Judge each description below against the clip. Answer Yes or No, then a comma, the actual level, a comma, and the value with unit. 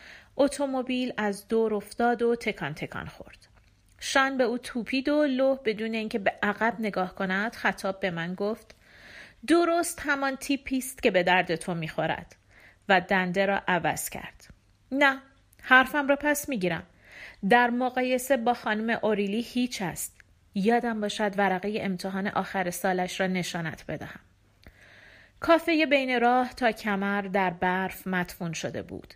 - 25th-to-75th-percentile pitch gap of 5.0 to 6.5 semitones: Yes, average, 5.3 semitones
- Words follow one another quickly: No, average, 140 wpm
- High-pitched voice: Yes, high, 215 Hz